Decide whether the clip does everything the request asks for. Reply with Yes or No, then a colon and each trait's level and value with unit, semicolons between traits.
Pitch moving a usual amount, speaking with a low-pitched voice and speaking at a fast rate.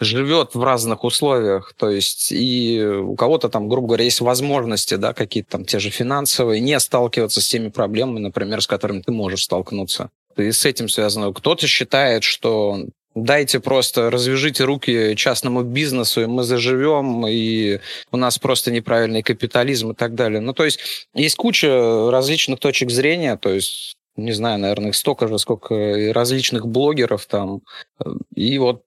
Yes: average, 3.4 semitones; low, 120 Hz; fast, 165 wpm